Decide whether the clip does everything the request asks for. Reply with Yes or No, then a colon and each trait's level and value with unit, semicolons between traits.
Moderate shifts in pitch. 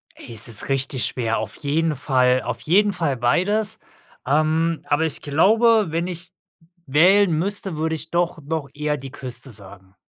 Yes: average, 5.0 semitones